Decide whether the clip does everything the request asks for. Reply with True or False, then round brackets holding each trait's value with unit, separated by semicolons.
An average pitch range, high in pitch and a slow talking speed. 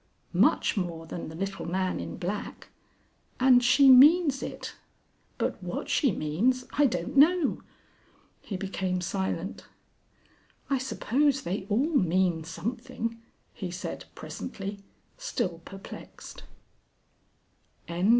False (6.3 semitones; 205 Hz; 115 wpm)